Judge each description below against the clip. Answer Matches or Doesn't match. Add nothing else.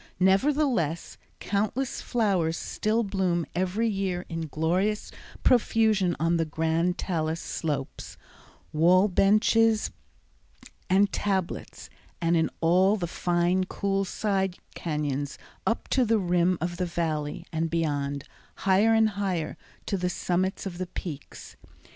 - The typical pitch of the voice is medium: Matches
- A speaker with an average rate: Doesn't match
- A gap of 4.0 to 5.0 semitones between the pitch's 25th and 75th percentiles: Doesn't match